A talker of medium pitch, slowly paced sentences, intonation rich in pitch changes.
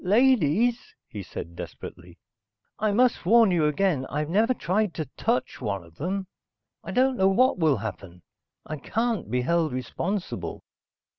No: medium, 180 Hz; average, 150 wpm; wide, 9.0 semitones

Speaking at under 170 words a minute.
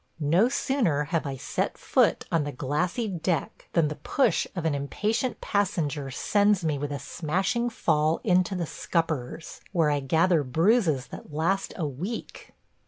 Yes: average, 160 wpm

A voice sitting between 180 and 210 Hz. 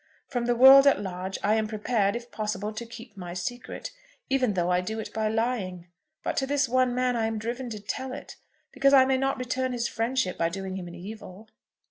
No: high, 225 Hz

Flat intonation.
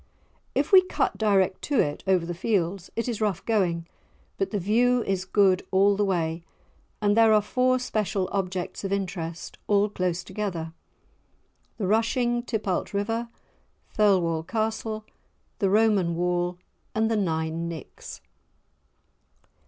No: average, 3.8 semitones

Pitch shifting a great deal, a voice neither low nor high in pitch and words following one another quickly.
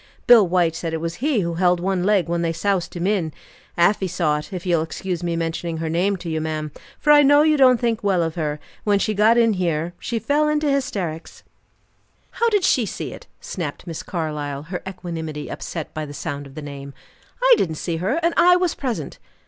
Yes: wide, 5.7 semitones; medium, 175 Hz; fast, 220 wpm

